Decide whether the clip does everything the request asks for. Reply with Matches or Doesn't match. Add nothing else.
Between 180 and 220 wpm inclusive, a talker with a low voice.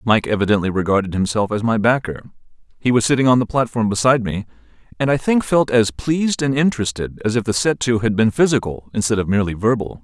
Matches